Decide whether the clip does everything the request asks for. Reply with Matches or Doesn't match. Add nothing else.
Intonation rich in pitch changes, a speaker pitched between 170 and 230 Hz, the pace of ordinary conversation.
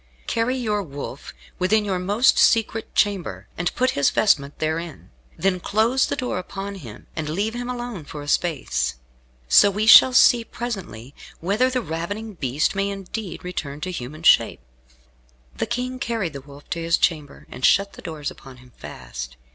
Matches